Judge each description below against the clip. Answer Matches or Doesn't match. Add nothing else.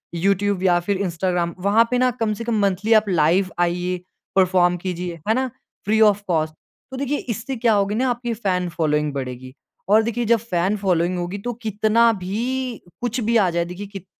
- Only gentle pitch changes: Doesn't match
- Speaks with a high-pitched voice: Matches